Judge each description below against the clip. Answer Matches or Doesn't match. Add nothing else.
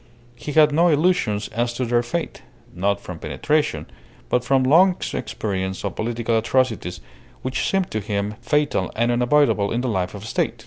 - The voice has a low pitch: Matches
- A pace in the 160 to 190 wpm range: Matches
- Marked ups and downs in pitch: Matches